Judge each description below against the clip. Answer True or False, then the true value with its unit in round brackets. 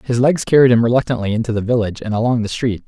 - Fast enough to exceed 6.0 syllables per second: True (7.3 syllables/s)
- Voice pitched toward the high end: False (115 Hz)